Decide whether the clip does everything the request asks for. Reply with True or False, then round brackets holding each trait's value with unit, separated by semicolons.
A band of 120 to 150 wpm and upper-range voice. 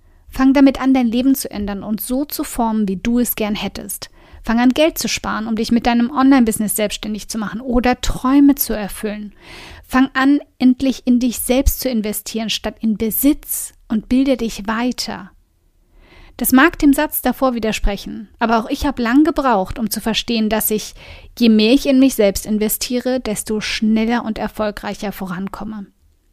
False (175 wpm; 230 Hz)